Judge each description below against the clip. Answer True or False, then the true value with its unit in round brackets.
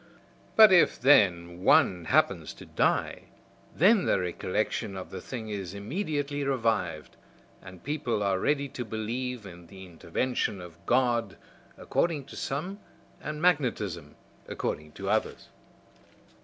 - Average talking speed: False (130 wpm)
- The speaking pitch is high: False (110 Hz)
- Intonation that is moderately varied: False (7.4 semitones)